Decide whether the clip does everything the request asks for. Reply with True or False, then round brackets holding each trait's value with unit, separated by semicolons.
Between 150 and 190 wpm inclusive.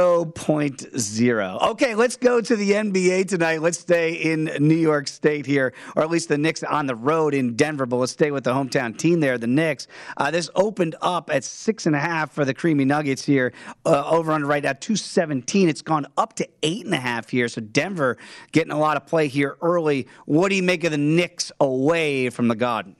False (205 wpm)